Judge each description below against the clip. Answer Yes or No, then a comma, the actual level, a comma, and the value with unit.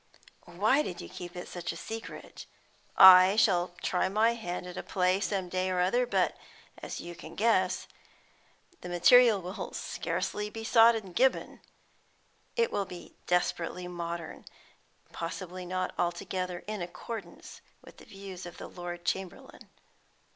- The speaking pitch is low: No, medium, 185 Hz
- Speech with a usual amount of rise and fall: Yes, average, 3.0 semitones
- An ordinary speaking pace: Yes, average, 150 wpm